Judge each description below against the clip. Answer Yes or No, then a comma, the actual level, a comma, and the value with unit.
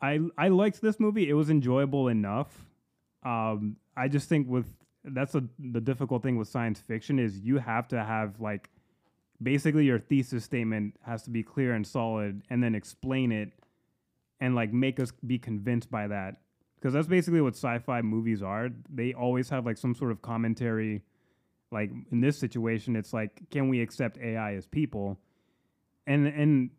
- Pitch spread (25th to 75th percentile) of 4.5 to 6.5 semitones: No, average, 3.6 semitones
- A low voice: Yes, low, 120 Hz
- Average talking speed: Yes, average, 175 wpm